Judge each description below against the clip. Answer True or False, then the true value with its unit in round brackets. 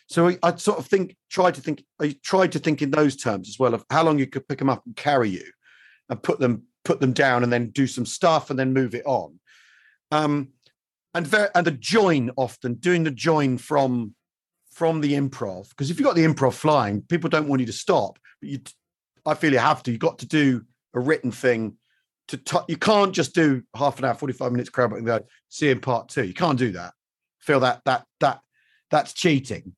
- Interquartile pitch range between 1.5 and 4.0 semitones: False (4.7 semitones)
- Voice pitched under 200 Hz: True (140 Hz)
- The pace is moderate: False (230 wpm)